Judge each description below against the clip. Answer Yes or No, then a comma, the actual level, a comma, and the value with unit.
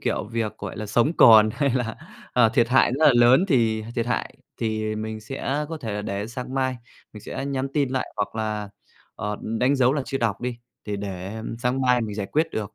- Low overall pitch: Yes, low, 115 Hz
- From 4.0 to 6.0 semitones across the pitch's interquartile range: No, average, 3.4 semitones